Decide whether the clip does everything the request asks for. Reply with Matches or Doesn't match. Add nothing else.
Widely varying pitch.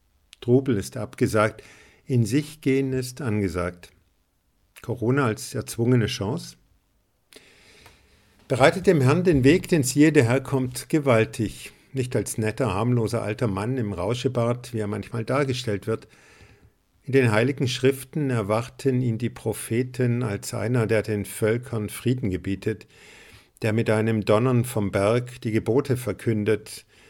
Doesn't match